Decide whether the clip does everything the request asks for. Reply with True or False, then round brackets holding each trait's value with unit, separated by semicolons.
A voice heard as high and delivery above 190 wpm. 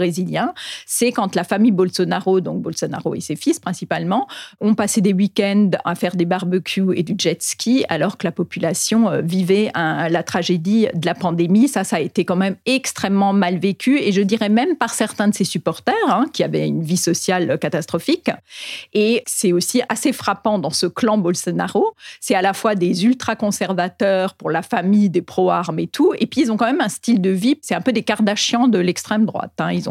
True (195 Hz; 205 wpm)